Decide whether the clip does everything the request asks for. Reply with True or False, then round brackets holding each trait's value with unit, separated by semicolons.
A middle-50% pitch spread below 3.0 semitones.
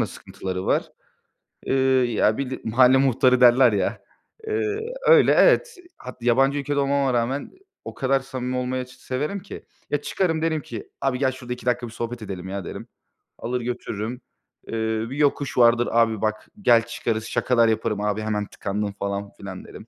False (3.7 semitones)